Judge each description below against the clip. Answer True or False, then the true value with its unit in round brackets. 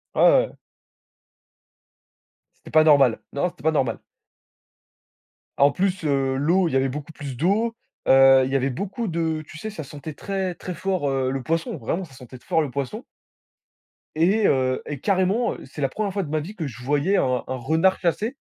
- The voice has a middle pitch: True (155 Hz)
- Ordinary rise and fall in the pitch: False (5.7 semitones)